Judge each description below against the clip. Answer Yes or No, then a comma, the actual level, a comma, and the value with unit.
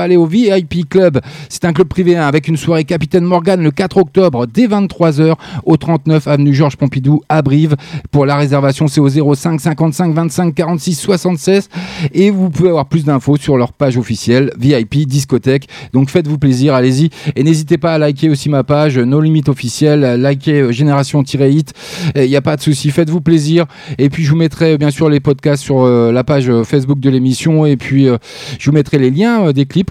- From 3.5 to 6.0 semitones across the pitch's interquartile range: No, average, 3.1 semitones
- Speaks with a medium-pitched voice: Yes, medium, 150 Hz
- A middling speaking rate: Yes, average, 200 wpm